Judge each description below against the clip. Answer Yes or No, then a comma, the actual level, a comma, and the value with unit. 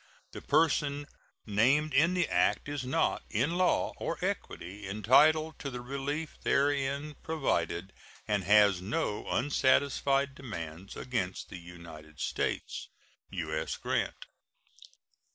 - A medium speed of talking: No, slow, 115 wpm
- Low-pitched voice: Yes, low, 130 Hz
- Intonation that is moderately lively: No, wide, 7.0 semitones